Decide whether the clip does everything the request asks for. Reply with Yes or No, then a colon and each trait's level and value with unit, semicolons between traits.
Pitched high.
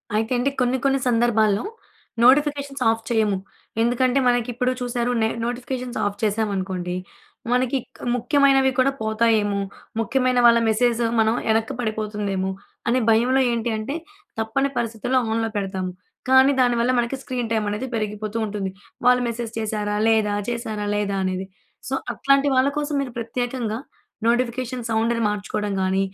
Yes: high, 230 Hz